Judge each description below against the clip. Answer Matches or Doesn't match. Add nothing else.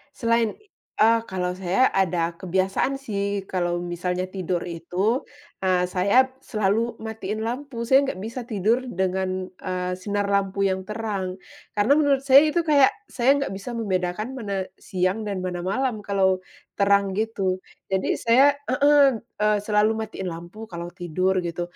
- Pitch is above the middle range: Matches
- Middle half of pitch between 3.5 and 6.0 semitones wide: Matches